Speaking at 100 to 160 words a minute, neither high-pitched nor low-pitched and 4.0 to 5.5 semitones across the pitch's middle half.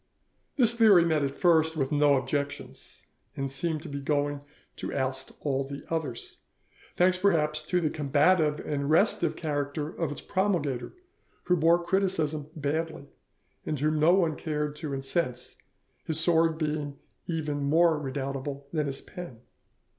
No: average, 145 wpm; medium, 150 Hz; average, 2.8 semitones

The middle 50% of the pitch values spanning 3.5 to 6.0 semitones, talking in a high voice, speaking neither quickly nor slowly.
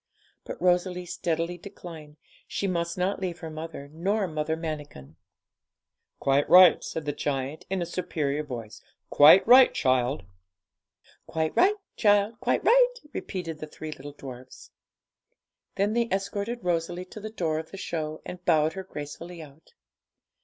No: average, 4.0 semitones; medium, 165 Hz; average, 145 wpm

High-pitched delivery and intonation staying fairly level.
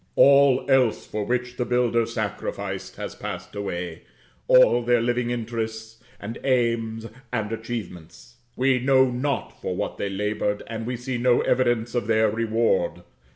No: low, 115 Hz; narrow, 2.1 semitones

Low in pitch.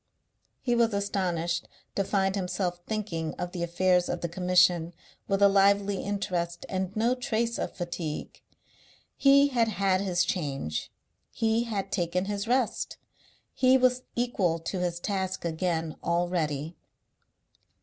No: medium, 185 Hz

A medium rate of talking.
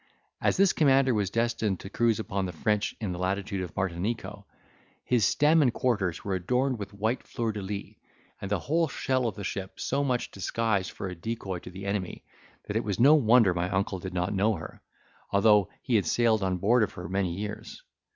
No: fast, 210 wpm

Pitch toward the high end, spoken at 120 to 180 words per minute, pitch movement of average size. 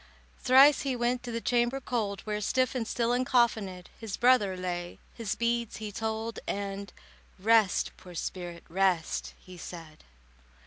Yes: high, 220 Hz; average, 145 wpm; average, 4.3 semitones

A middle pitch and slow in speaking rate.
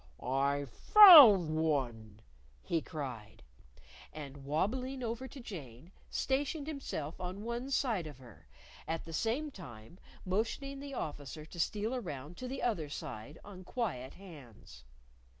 Yes: medium, 170 Hz; slow, 130 wpm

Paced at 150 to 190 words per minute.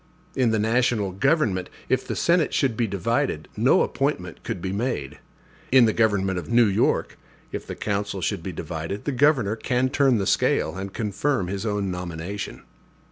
Yes: average, 175 wpm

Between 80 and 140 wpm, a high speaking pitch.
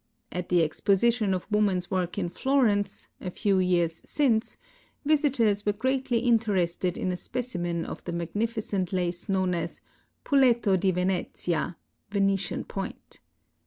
Yes: slow, 135 wpm; high, 195 Hz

